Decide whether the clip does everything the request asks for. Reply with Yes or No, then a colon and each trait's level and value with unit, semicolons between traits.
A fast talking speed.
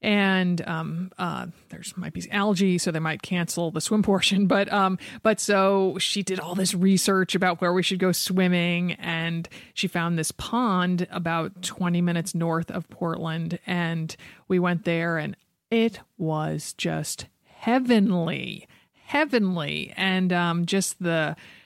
No: average, 150 wpm